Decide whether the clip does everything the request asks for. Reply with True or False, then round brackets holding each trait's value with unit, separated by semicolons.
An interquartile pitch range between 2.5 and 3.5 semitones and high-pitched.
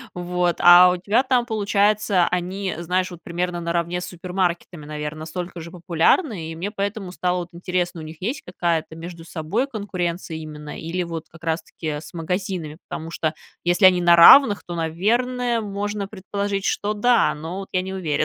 False (3.1 semitones; 180 Hz)